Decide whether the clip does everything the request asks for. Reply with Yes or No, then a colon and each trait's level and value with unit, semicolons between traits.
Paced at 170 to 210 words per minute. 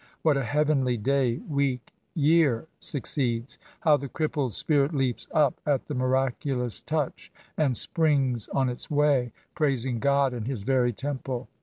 No: average, 145 wpm